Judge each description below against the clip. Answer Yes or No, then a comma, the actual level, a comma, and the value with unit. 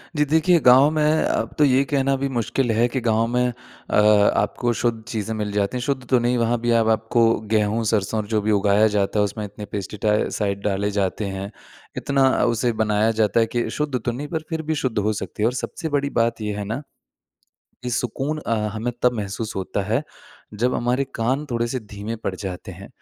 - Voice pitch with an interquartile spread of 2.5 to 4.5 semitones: Yes, average, 3.6 semitones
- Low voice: Yes, low, 115 Hz